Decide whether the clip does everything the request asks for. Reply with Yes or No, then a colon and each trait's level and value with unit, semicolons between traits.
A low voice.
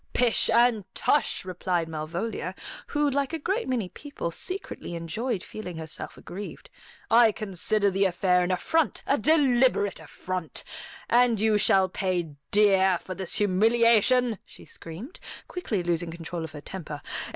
No: high, 200 Hz